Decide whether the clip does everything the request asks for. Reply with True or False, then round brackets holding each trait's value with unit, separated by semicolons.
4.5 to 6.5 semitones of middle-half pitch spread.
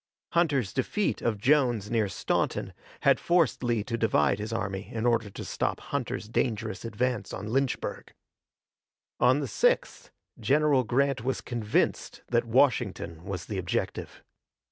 False (4.1 semitones)